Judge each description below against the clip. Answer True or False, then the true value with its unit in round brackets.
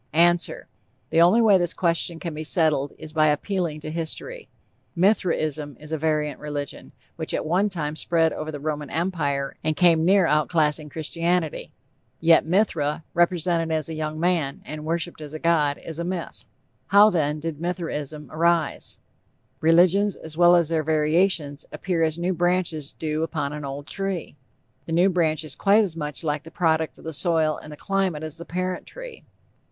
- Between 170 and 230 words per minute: True (175 wpm)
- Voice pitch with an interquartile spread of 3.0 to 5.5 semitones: False (2.4 semitones)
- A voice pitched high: False (160 Hz)